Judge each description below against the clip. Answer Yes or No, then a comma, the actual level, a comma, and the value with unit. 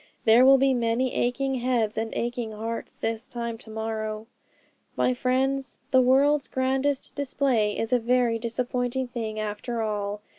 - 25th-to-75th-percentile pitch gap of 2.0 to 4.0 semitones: Yes, average, 2.7 semitones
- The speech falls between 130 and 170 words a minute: Yes, average, 150 wpm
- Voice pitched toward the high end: Yes, high, 240 Hz